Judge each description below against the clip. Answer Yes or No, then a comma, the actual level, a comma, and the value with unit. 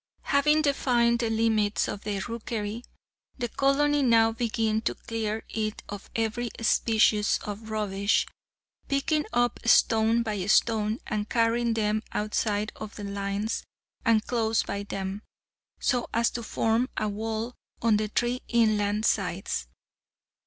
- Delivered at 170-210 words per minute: No, slow, 135 wpm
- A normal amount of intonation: No, narrow, 2.0 semitones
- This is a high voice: Yes, high, 220 Hz